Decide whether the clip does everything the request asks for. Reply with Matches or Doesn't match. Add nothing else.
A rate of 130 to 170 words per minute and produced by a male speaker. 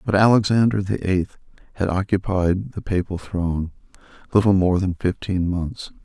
Matches